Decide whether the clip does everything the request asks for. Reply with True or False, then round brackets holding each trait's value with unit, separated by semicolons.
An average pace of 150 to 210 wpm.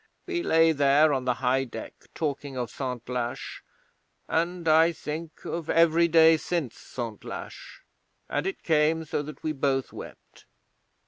False (140 wpm)